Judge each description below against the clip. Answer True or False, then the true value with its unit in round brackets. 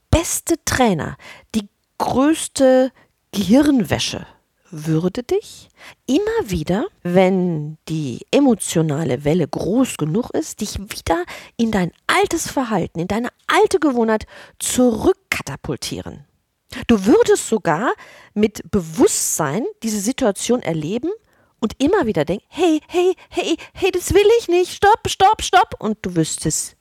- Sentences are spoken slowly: True (120 wpm)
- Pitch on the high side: True (235 Hz)